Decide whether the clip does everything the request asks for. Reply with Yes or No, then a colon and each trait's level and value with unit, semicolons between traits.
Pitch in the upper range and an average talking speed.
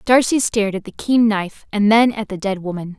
No: high, 210 Hz; fast, 240 wpm